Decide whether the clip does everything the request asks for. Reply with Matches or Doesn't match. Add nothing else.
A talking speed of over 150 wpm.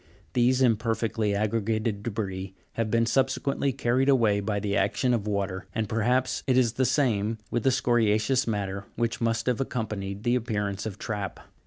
Matches